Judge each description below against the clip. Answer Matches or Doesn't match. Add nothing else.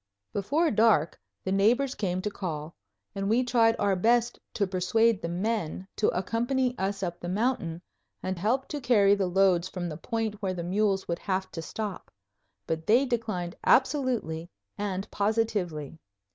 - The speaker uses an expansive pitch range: Doesn't match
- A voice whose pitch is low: Doesn't match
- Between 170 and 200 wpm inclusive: Doesn't match